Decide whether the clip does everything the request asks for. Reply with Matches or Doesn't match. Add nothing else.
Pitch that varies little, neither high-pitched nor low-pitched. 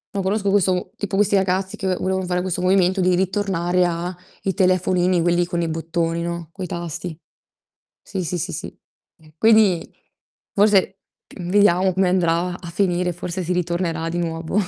Matches